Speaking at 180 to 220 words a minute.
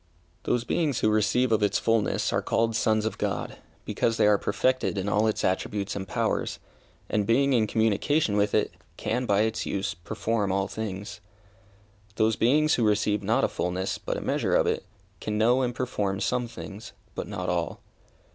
Yes: average, 185 wpm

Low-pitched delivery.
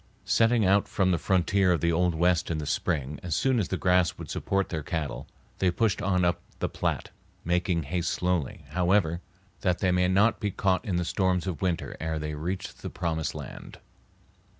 Yes: very low, 90 Hz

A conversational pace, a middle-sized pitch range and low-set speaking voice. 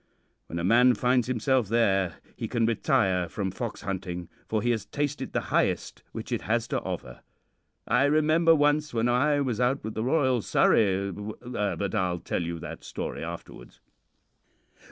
Yes: average, 165 wpm; average, 5.0 semitones; low, 115 Hz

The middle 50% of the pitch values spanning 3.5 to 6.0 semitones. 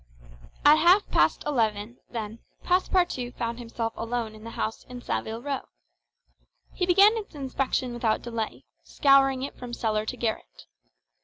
Yes: average, 3.8 semitones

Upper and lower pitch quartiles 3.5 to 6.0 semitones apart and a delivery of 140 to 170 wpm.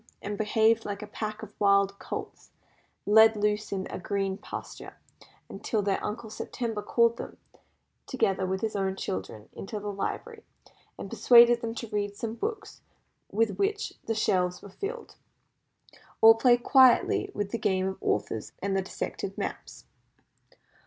No: average, 2.8 semitones; average, 160 wpm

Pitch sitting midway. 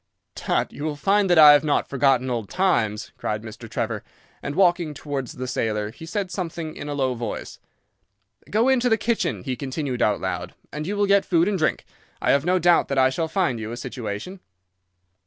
Yes: medium, 145 Hz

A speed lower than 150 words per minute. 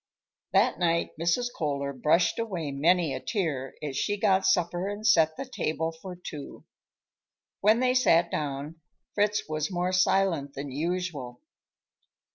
Yes: average, 140 wpm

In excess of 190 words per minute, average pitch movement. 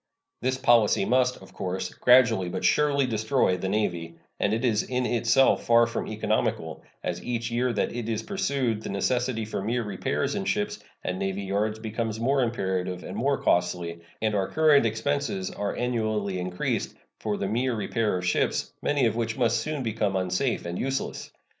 No: average, 180 wpm; average, 4.2 semitones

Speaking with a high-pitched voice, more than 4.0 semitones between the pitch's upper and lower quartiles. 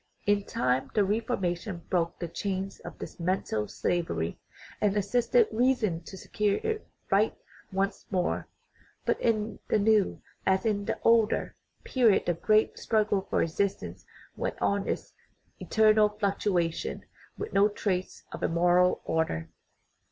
No: high, 200 Hz; average, 3.4 semitones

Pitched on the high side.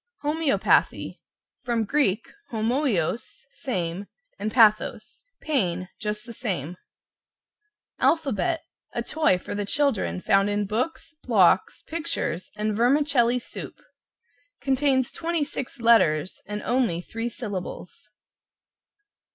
Yes: high, 230 Hz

